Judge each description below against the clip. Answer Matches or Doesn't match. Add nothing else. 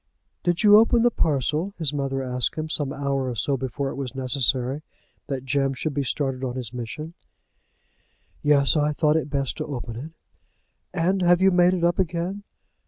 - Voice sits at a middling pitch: Matches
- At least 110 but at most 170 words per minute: Doesn't match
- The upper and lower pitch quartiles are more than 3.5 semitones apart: Matches